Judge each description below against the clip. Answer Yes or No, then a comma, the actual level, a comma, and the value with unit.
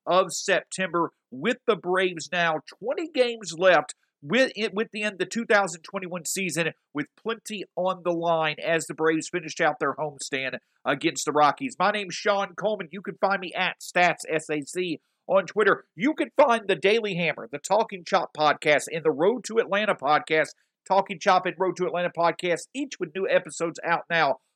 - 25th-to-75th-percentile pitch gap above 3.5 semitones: Yes, average, 3.9 semitones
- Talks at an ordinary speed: Yes, average, 180 wpm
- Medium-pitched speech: Yes, medium, 180 Hz